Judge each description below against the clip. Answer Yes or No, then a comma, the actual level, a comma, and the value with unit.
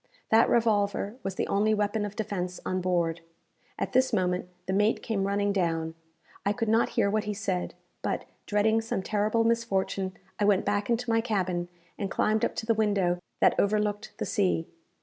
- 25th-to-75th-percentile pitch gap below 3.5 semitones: Yes, narrow, 2.5 semitones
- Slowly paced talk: No, average, 185 wpm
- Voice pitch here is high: Yes, high, 205 Hz